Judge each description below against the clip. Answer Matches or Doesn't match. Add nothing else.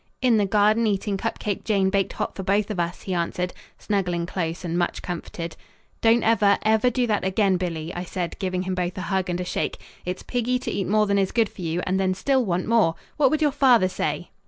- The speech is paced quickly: Matches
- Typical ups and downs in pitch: Matches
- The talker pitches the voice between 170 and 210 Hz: Matches